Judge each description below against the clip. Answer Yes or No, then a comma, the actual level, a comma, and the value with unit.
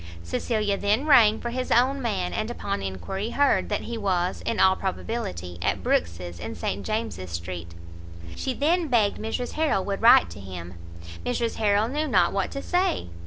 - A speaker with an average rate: Yes, average, 175 wpm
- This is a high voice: Yes, high, 205 Hz